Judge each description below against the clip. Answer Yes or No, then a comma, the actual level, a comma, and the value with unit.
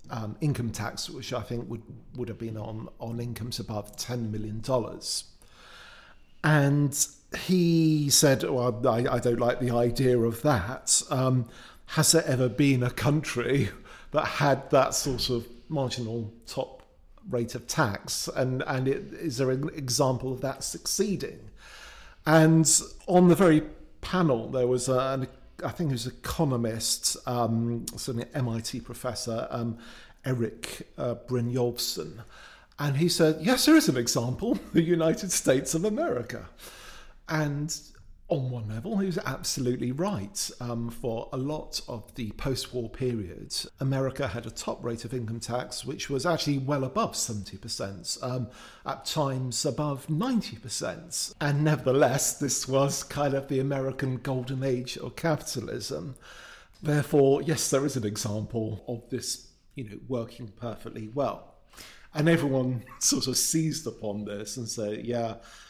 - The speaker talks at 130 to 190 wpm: Yes, average, 150 wpm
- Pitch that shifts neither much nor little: Yes, average, 3.5 semitones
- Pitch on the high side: No, low, 130 Hz